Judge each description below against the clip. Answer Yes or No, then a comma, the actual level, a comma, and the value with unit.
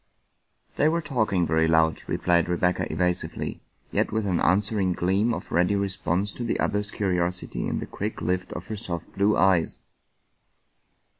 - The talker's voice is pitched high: No, very low, 95 Hz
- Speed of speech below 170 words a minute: Yes, average, 160 wpm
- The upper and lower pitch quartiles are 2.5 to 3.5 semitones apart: Yes, average, 2.8 semitones